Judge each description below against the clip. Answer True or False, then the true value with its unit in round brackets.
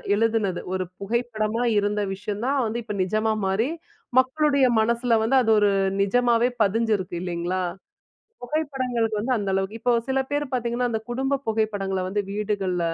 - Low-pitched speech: False (220 Hz)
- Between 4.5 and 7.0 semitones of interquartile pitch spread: False (3.3 semitones)